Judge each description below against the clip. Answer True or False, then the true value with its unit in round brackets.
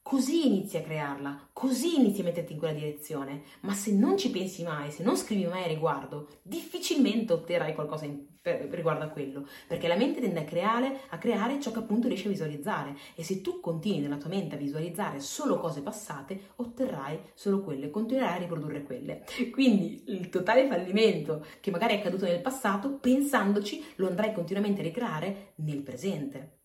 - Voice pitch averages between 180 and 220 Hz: True (185 Hz)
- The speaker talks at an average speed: False (180 wpm)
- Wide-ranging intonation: True (6.6 semitones)